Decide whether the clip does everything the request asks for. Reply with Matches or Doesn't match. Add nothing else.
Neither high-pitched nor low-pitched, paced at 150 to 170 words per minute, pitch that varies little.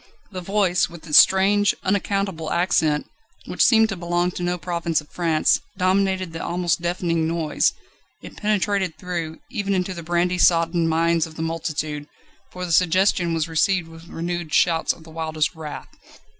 Matches